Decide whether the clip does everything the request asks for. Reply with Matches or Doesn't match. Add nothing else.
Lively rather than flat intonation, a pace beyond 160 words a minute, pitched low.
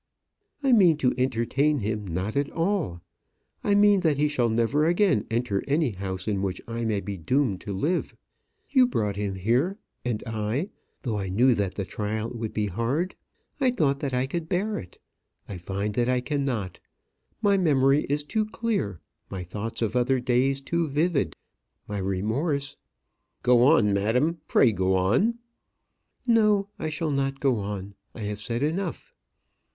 Matches